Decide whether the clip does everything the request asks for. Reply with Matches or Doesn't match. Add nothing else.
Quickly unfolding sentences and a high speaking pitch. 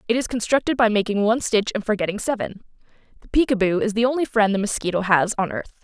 Matches